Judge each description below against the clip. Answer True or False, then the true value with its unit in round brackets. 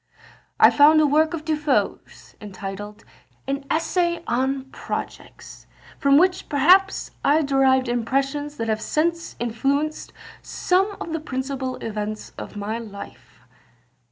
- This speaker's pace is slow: True (130 wpm)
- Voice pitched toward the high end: True (275 Hz)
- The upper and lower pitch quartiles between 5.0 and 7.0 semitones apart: False (4.6 semitones)